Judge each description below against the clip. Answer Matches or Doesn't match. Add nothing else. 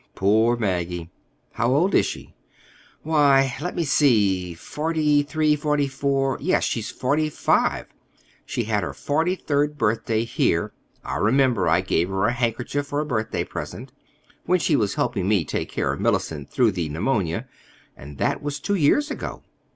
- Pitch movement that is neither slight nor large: Doesn't match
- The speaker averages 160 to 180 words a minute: Doesn't match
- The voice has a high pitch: Doesn't match